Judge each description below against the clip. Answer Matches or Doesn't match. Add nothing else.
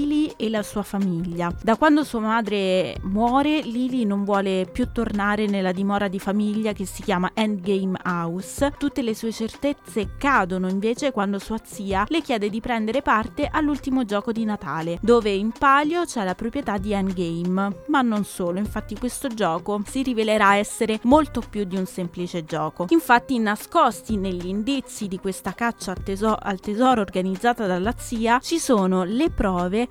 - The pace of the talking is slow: Doesn't match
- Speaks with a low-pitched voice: Doesn't match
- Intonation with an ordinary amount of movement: Matches